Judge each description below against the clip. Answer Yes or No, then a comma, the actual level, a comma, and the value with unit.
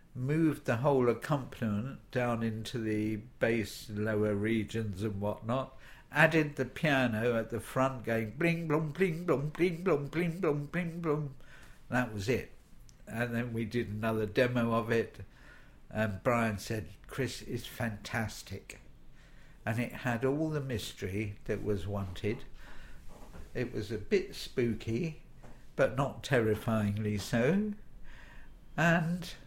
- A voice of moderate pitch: No, low, 120 Hz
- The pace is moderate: No, slow, 130 wpm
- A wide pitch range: No, average, 4.8 semitones